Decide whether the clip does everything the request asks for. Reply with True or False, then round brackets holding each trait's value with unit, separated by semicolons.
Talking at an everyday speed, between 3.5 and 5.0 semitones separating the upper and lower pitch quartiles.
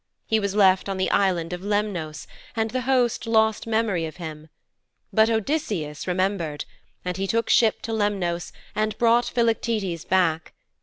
True (155 wpm; 4.1 semitones)